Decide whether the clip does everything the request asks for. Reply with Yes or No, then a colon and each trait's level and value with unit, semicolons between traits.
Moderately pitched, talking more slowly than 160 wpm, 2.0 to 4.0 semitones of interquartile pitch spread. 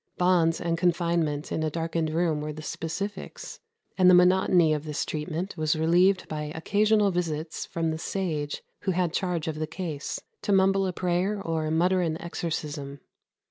No: medium, 170 Hz; average, 170 wpm; average, 2.7 semitones